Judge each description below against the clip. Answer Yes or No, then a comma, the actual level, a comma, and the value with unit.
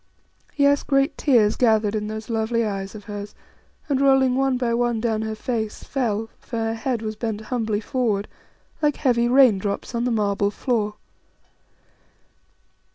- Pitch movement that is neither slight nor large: Yes, average, 3.0 semitones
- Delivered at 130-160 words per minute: Yes, average, 155 wpm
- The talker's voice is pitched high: Yes, high, 225 Hz